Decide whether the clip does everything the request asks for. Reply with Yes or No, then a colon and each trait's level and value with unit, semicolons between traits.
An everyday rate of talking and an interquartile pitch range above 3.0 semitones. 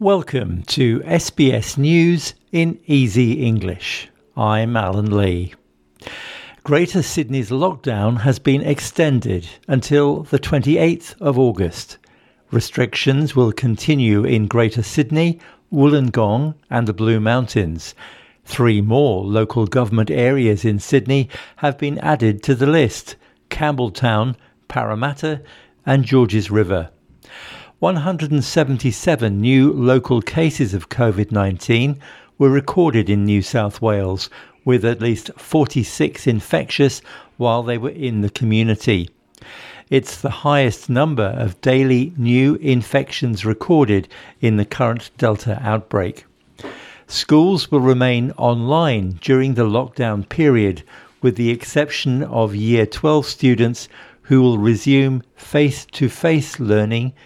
No: slow, 115 wpm; average, 4.6 semitones